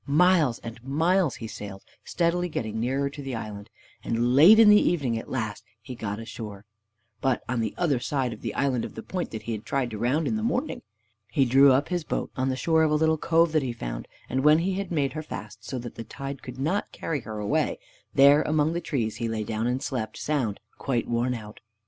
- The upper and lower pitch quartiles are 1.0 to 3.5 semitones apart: No, wide, 5.4 semitones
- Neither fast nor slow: No, fast, 225 wpm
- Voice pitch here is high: No, low, 130 Hz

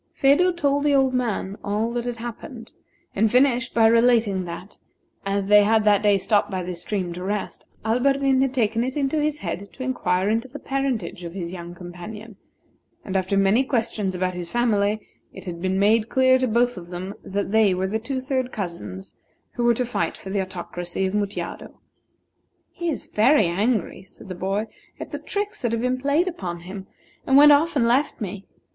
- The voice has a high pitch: Yes, high, 215 Hz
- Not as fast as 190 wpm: No, average, 200 wpm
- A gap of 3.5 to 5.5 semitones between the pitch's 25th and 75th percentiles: Yes, average, 5.2 semitones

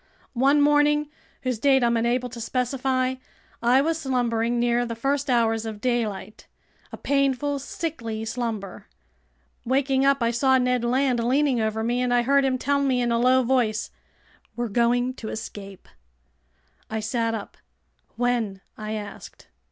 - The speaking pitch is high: Yes, high, 245 Hz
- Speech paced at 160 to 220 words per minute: No, average, 145 wpm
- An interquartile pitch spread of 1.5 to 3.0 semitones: Yes, narrow, 2.6 semitones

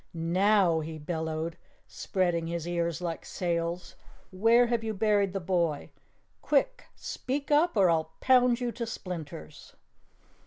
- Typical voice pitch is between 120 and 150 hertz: No, medium, 180 Hz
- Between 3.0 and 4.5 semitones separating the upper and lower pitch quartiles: No, average, 5.3 semitones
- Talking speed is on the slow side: Yes, slow, 130 wpm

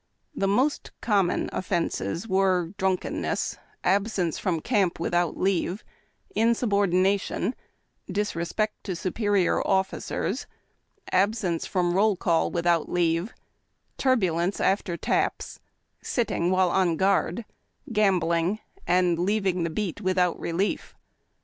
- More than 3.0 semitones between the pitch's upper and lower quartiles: No, average, 2.7 semitones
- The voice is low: No, medium, 185 Hz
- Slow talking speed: Yes, slow, 105 wpm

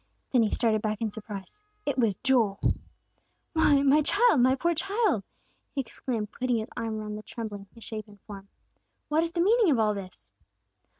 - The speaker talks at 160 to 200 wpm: Yes, average, 175 wpm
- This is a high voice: Yes, high, 230 Hz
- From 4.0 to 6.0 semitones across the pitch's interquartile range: Yes, wide, 5.4 semitones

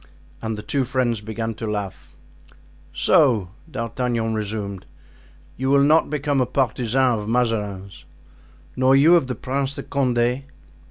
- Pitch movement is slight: No, average, 3.5 semitones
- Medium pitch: No, low, 120 Hz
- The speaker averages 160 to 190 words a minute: No, average, 140 wpm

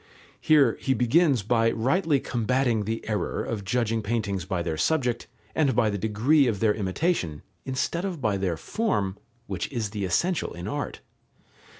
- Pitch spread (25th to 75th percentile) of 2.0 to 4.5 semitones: No, average, 5.2 semitones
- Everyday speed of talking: Yes, average, 165 wpm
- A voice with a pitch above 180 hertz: No, low, 115 Hz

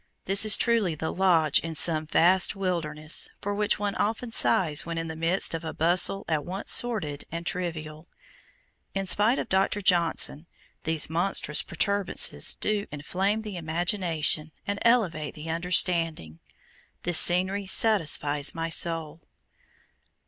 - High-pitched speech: No, medium, 170 Hz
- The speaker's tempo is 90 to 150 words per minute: Yes, average, 140 wpm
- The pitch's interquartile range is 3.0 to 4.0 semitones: Yes, average, 3.6 semitones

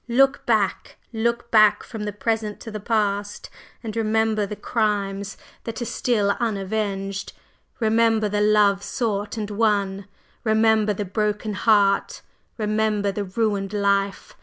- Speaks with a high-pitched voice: Yes, high, 210 Hz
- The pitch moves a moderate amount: No, narrow, 1.7 semitones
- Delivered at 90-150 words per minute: Yes, slow, 135 wpm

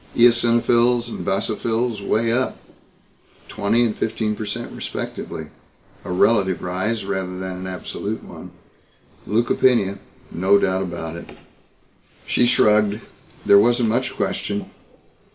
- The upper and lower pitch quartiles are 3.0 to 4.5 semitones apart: Yes, average, 3.6 semitones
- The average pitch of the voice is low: Yes, low, 105 Hz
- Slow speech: Yes, slow, 115 wpm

